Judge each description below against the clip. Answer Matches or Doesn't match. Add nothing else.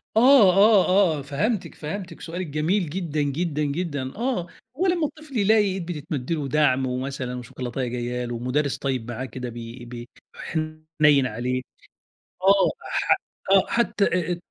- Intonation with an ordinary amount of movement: Doesn't match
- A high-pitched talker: Doesn't match